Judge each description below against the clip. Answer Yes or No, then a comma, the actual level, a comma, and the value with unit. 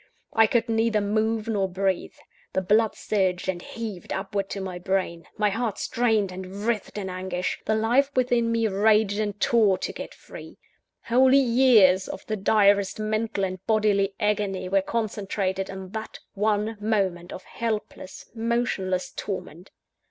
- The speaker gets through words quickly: No, average, 150 wpm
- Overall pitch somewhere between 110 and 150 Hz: No, high, 205 Hz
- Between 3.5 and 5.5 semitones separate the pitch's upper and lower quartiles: No, average, 2.7 semitones